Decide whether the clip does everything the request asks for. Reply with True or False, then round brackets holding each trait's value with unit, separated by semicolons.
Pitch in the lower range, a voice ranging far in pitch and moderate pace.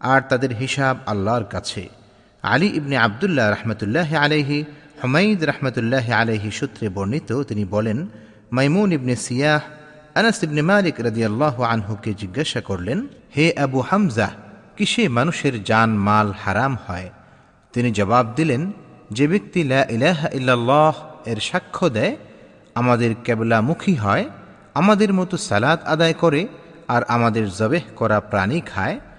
True (130 Hz; 6.1 semitones; 110 wpm)